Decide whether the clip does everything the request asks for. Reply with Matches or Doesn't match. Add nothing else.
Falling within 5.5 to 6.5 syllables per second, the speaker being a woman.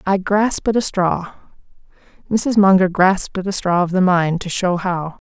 Doesn't match